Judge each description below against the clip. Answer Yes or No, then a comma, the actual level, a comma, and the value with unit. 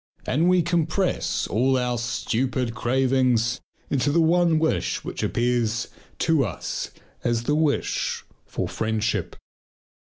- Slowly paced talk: Yes, slow, 120 wpm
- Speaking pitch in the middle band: No, low, 130 Hz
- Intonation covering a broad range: No, average, 5.0 semitones